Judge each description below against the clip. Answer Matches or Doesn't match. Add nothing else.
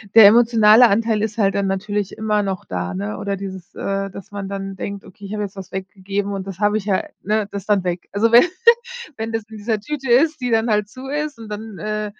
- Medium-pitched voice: Doesn't match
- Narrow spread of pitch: Matches